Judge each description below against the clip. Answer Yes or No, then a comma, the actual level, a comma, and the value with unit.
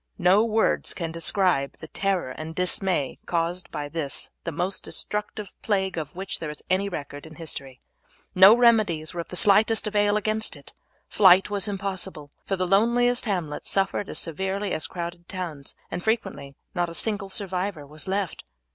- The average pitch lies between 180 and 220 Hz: Yes, medium, 185 Hz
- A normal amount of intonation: Yes, average, 3.8 semitones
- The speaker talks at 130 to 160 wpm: No, average, 170 wpm